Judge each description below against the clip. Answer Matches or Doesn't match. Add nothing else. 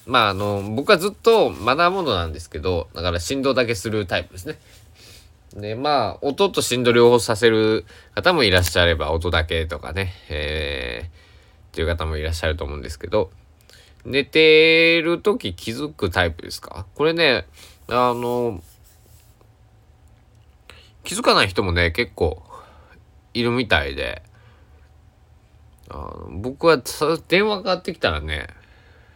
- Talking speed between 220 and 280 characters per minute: Matches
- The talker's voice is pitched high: Doesn't match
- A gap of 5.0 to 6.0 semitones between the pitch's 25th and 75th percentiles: Doesn't match